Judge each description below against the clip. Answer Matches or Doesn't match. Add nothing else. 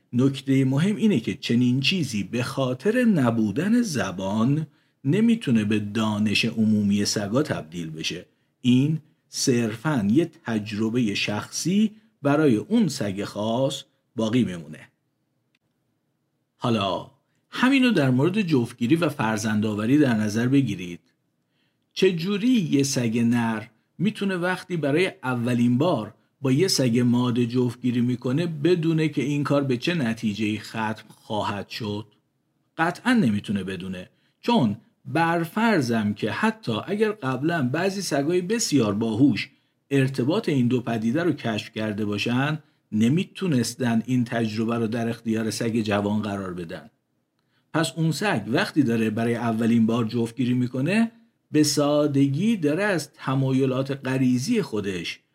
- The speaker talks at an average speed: Matches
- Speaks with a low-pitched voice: Matches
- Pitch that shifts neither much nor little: Doesn't match